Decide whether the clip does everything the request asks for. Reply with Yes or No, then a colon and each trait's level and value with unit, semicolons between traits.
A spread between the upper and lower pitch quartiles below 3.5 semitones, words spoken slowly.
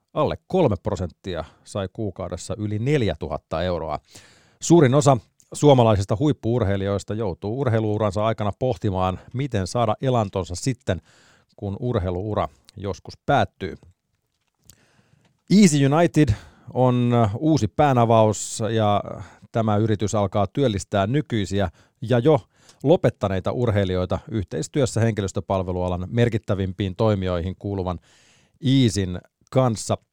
No: average, 4.1 semitones; slow, 90 wpm